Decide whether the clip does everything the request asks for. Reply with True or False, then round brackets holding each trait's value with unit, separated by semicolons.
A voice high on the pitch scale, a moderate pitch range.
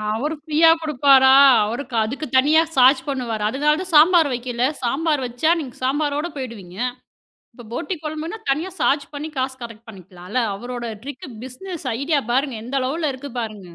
True (265 Hz; 4.0 semitones)